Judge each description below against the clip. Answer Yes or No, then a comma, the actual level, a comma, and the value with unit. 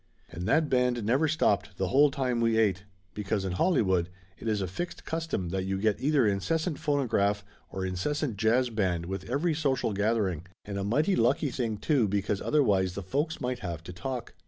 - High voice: No, low, 110 Hz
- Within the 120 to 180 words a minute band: No, average, 190 wpm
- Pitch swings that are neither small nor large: No, wide, 6.2 semitones